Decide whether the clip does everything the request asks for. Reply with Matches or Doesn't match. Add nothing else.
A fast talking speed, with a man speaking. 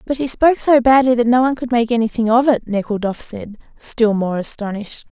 Doesn't match